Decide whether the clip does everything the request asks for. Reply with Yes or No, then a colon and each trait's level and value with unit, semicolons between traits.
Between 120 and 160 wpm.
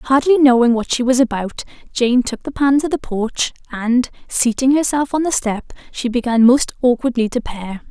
No: average, 190 wpm